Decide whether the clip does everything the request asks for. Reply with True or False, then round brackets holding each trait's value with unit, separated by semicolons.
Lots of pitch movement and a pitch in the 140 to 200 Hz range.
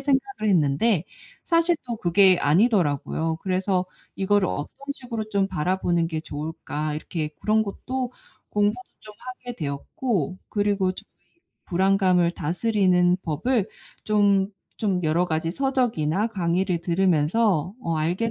False (4.4 semitones; 190 Hz)